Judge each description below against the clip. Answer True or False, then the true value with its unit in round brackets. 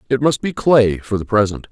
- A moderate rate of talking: False (245 wpm)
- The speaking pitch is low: True (115 Hz)